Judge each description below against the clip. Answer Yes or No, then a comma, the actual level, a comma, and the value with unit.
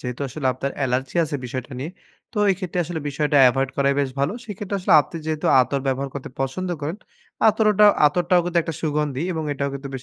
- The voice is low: No, medium, 145 Hz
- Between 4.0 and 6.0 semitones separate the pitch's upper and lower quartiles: Yes, average, 4.4 semitones